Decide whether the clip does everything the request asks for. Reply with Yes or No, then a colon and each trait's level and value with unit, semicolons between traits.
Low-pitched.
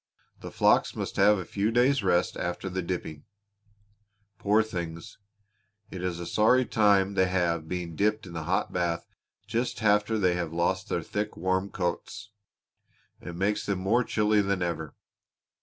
Yes: very low, 95 Hz